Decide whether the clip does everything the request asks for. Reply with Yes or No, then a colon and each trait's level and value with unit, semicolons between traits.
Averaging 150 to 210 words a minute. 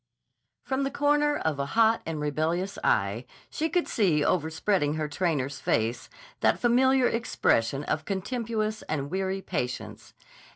No: slow, 135 wpm